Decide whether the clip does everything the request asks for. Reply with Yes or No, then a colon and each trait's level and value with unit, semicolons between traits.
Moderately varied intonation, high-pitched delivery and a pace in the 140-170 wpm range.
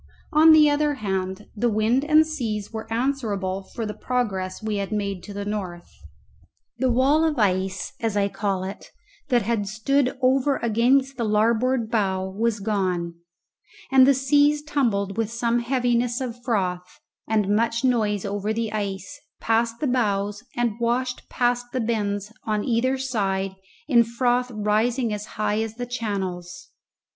Yes: average, 3.6 semitones; high, 225 Hz; average, 155 wpm